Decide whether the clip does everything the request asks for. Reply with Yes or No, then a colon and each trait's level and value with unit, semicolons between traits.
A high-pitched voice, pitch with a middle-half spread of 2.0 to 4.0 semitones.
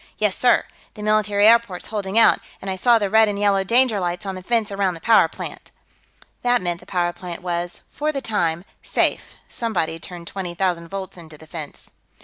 Yes: high, 195 Hz; average, 3.7 semitones